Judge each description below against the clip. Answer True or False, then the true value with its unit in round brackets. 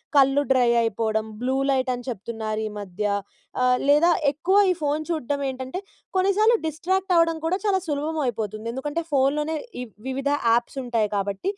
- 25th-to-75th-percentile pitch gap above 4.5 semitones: True (5.6 semitones)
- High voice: True (270 Hz)